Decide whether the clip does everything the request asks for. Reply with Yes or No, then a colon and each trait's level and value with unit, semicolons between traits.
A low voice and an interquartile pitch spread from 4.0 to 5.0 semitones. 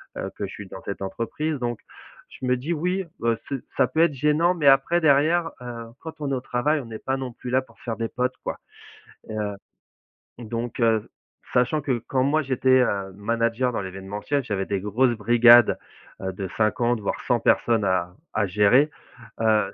Yes: low, 120 Hz; average, 4.4 semitones